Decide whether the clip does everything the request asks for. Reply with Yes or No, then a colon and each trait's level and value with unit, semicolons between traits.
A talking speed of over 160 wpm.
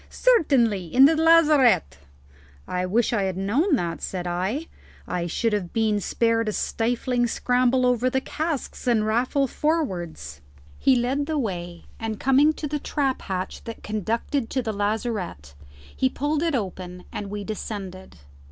No: average, 155 wpm